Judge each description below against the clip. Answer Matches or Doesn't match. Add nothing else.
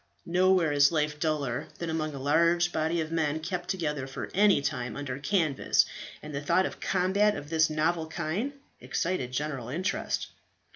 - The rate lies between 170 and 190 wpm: Matches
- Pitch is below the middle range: Doesn't match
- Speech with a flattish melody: Doesn't match